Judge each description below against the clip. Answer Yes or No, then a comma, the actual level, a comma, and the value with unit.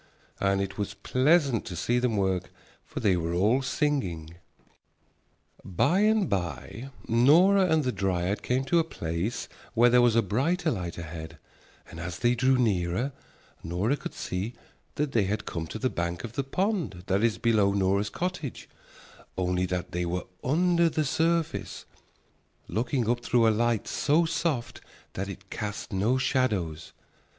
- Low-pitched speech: Yes, low, 115 Hz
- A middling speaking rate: Yes, average, 160 wpm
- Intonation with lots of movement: Yes, wide, 6.8 semitones